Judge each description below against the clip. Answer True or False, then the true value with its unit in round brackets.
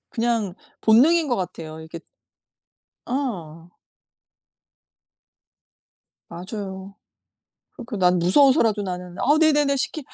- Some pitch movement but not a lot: False (6.8 semitones)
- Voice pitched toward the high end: True (205 Hz)